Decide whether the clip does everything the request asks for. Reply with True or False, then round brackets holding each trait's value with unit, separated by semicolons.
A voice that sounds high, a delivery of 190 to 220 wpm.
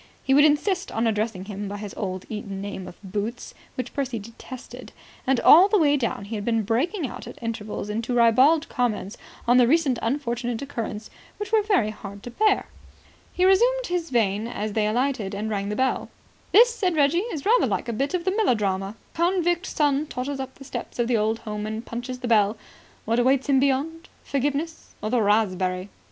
True (245 Hz; 200 wpm)